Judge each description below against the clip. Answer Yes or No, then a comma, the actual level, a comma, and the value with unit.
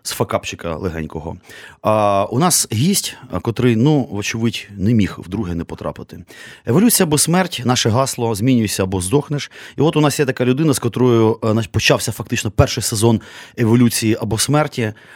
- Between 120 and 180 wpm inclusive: Yes, fast, 155 wpm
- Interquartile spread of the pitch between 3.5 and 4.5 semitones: Yes, average, 4.0 semitones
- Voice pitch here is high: No, low, 115 Hz